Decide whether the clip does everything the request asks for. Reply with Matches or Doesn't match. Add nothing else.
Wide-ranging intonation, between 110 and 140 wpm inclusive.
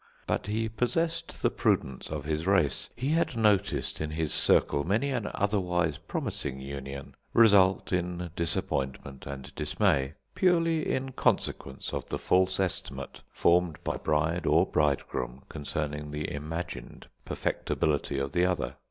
Matches